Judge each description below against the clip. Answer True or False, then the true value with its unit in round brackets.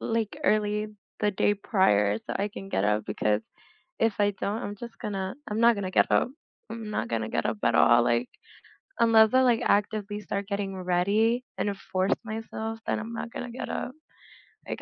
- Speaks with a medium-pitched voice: False (205 Hz)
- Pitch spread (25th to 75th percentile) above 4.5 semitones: False (3.0 semitones)